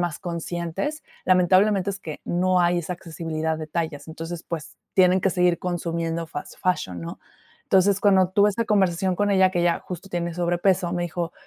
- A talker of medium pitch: Yes, medium, 175 Hz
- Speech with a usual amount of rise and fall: No, narrow, 2.1 semitones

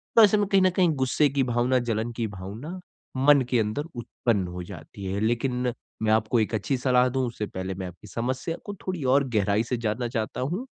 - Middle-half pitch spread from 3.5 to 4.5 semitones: Yes, average, 4.1 semitones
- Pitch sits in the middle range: No, low, 120 Hz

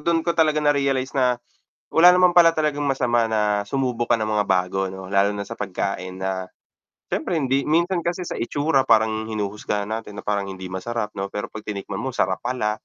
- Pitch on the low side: Yes, low, 115 Hz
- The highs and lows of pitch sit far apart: Yes, wide, 6.0 semitones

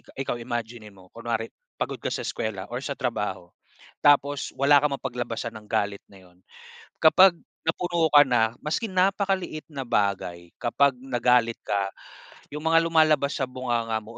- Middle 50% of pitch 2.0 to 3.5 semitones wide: No, average, 4.7 semitones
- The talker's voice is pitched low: Yes, low, 125 Hz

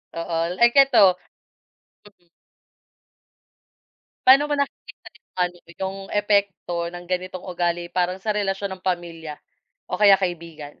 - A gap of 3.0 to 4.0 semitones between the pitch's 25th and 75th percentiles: No, narrow, 2.6 semitones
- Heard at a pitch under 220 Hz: Yes, medium, 185 Hz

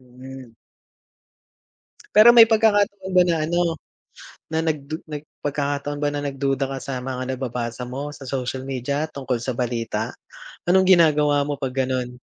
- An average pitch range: Yes, average, 3.4 semitones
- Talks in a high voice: No, medium, 140 Hz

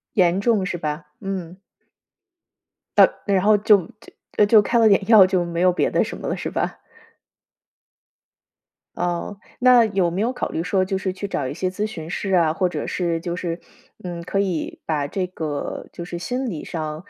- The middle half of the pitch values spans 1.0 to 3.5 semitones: Yes, average, 2.9 semitones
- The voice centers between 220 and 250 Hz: No, medium, 185 Hz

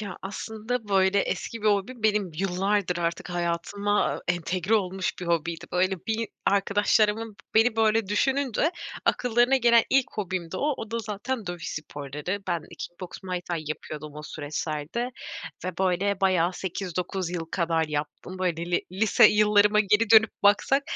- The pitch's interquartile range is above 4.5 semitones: No, average, 3.8 semitones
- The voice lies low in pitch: No, high, 195 Hz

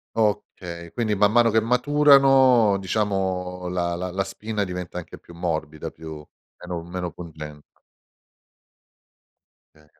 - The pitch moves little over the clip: No, average, 4.1 semitones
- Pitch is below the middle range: Yes, very low, 90 Hz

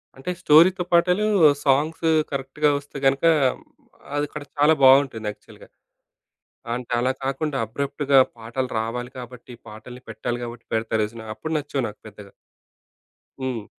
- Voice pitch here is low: Yes, low, 130 Hz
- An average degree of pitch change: Yes, average, 3.9 semitones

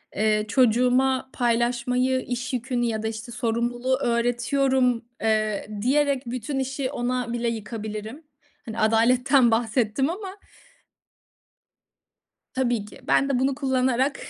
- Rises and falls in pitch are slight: Yes, narrow, 2.3 semitones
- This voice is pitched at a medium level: No, high, 245 Hz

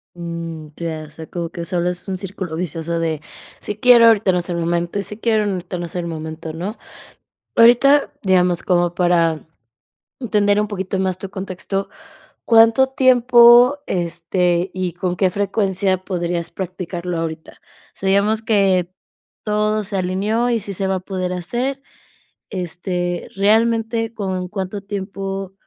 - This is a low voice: No, high, 190 Hz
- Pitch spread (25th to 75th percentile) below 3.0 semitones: No, average, 3.3 semitones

